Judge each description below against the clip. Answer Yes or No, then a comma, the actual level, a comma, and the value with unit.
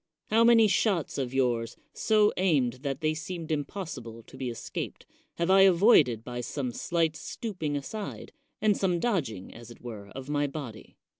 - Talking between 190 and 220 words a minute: No, average, 165 wpm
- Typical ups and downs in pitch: No, wide, 7.3 semitones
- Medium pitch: Yes, medium, 150 Hz